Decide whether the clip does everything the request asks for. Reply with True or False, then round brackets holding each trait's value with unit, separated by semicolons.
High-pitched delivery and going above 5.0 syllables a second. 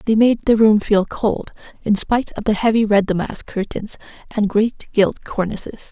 False (210 Hz; 4.7 syllables/s)